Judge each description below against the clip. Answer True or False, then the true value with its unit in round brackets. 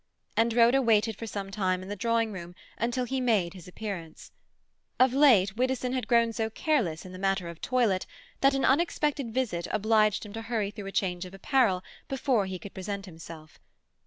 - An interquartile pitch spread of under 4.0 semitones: False (4.6 semitones)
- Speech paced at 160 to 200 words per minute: True (190 wpm)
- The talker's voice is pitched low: False (215 Hz)